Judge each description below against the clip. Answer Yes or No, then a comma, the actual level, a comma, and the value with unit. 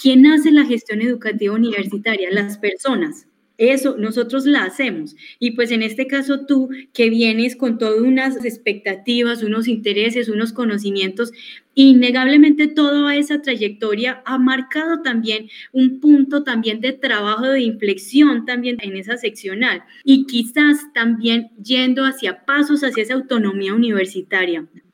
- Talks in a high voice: Yes, high, 245 Hz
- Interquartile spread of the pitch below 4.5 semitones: Yes, average, 3.7 semitones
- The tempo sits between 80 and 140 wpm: Yes, average, 135 wpm